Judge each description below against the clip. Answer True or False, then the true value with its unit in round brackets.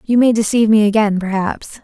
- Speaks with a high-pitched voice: True (215 Hz)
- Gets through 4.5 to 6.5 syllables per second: True (5.8 syllables/s)